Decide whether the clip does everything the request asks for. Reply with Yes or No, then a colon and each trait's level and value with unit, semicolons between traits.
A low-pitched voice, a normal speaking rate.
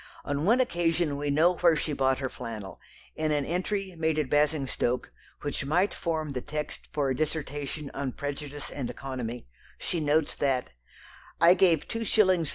No: medium, 150 Hz; average, 165 wpm